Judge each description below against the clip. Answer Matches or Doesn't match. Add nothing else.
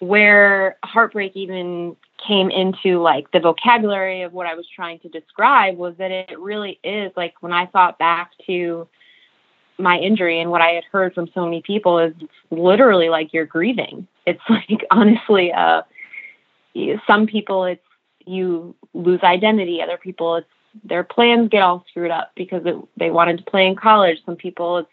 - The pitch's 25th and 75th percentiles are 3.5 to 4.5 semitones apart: Doesn't match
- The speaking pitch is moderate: Matches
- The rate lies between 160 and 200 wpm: Matches